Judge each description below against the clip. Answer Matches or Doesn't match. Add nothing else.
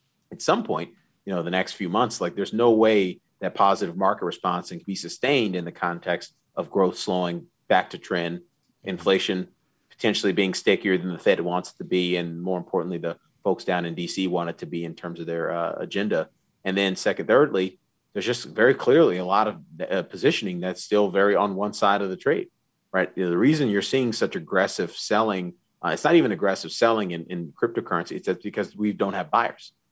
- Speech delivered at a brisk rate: Matches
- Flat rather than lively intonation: Matches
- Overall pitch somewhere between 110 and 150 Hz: Doesn't match